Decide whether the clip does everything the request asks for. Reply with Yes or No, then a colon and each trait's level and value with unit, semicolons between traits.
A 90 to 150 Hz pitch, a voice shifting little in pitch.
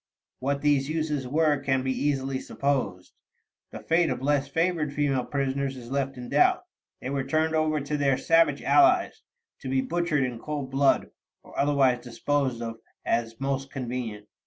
Yes: medium, 140 Hz; narrow, 2.2 semitones